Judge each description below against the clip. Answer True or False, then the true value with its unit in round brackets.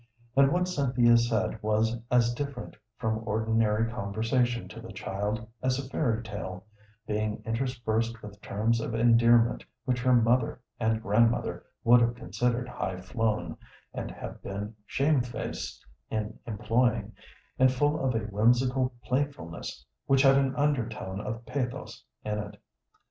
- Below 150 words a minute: True (140 wpm)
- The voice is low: True (115 Hz)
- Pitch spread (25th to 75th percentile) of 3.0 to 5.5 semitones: False (2.6 semitones)